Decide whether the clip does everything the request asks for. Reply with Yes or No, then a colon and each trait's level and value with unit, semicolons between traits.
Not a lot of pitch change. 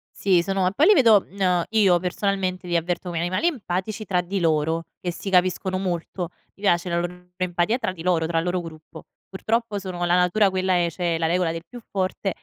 Yes: narrow, 2.1 semitones